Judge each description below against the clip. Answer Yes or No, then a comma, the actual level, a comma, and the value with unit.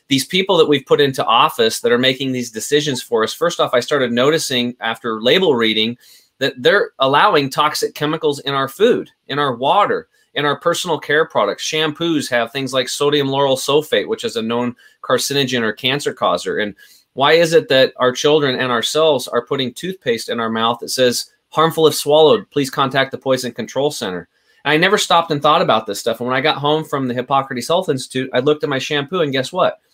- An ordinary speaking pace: No, fast, 210 wpm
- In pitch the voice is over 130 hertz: Yes, medium, 140 Hz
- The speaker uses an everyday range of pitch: Yes, average, 3.4 semitones